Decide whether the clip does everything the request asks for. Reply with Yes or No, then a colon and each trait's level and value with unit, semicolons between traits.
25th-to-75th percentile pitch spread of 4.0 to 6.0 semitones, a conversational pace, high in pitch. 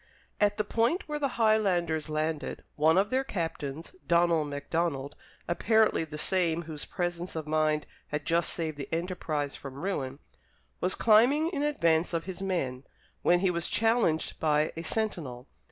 No: average, 4.8 semitones; average, 155 wpm; medium, 170 Hz